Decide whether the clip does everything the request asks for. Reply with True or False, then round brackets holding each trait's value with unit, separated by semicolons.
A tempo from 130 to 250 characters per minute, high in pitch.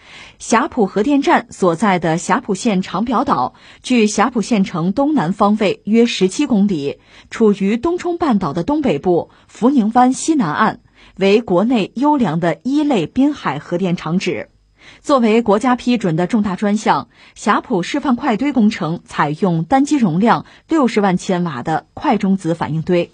True (245 characters per minute; 210 Hz)